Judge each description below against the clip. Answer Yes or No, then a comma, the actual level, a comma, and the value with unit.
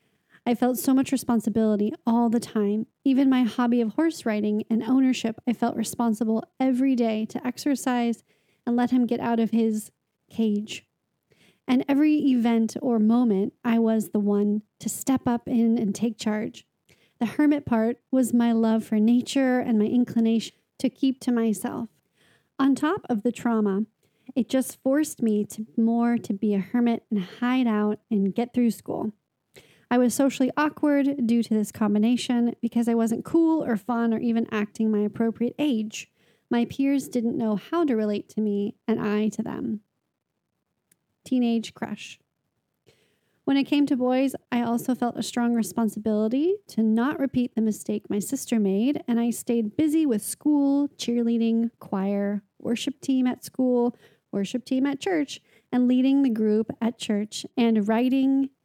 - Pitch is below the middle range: No, high, 235 Hz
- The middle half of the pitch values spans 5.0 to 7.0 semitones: No, average, 2.8 semitones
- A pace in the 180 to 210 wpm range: No, average, 165 wpm